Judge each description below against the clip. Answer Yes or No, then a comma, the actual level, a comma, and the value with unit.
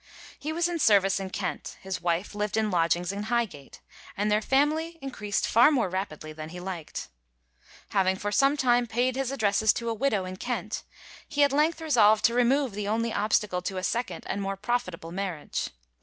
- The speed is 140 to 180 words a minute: No, average, 190 wpm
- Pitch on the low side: No, high, 210 Hz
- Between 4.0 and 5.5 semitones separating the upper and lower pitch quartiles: Yes, average, 4.7 semitones